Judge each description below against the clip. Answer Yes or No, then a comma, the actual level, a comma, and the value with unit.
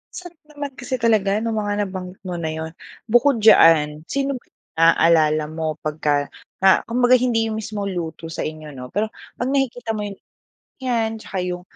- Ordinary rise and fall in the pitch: No, wide, 6.5 semitones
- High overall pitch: Yes, high, 205 Hz